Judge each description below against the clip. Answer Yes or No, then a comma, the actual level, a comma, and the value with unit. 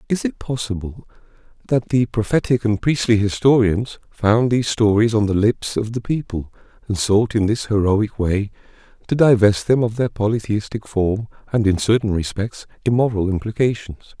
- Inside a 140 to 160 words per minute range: Yes, average, 155 wpm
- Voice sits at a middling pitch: No, low, 110 Hz